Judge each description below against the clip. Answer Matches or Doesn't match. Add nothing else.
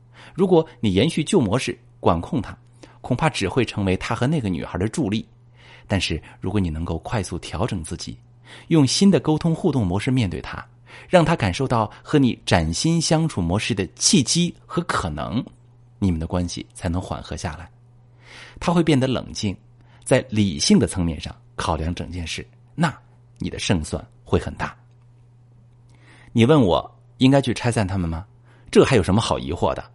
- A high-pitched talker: Doesn't match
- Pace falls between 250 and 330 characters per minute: Matches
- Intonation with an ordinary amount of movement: Matches